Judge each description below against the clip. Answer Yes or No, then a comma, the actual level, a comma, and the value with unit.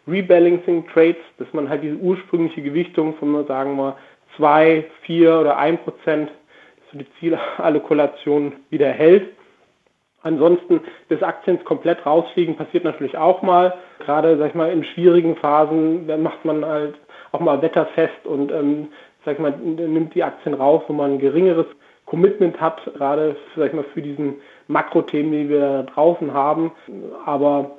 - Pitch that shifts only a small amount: Yes, narrow, 2.3 semitones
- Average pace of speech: Yes, average, 160 wpm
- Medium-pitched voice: Yes, medium, 155 Hz